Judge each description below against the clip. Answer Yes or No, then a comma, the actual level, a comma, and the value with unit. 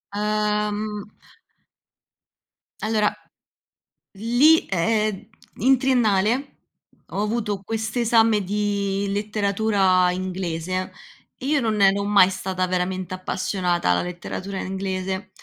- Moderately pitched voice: No, high, 200 Hz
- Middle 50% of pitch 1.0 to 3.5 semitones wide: Yes, narrow, 2.5 semitones